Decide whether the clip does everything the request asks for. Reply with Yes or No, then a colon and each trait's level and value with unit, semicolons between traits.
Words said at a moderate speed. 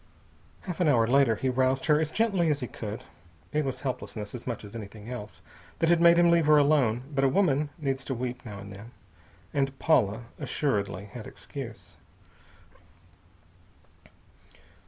Yes: average, 165 wpm